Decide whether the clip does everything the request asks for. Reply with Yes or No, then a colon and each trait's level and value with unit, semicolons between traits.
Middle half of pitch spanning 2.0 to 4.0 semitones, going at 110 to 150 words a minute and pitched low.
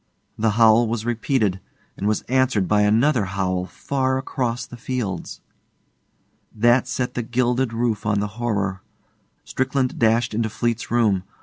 Yes: average, 3.0 semitones; average, 140 wpm; low, 115 Hz